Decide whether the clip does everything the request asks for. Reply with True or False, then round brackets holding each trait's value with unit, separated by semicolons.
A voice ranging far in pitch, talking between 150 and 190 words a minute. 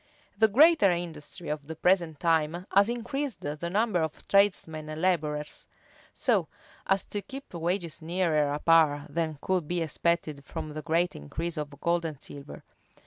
False (3.6 semitones; 160 wpm)